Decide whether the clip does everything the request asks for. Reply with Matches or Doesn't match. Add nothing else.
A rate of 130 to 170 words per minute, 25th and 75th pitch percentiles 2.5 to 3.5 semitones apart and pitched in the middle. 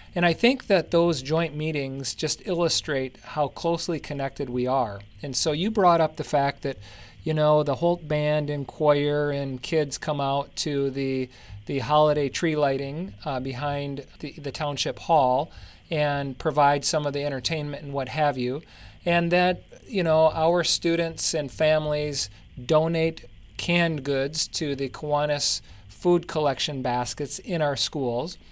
Matches